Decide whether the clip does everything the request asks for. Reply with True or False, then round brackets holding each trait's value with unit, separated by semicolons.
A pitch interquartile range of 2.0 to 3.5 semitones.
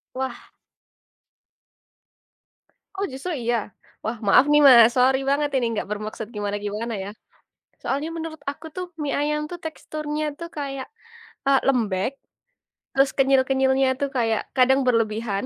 False (4.1 semitones)